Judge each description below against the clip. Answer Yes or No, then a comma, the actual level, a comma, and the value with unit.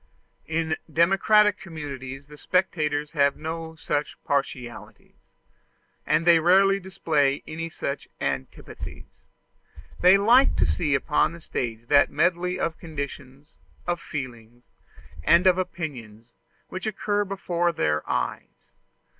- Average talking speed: No, slow, 115 wpm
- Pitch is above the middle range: No, medium, 160 Hz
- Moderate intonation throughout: Yes, average, 4.7 semitones